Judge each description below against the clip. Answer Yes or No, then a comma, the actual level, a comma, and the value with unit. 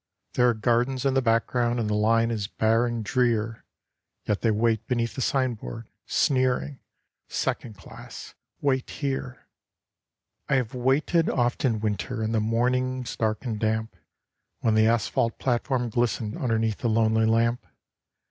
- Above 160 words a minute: No, average, 150 wpm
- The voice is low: Yes, low, 115 Hz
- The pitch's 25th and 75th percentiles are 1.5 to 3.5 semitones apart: Yes, narrow, 2.4 semitones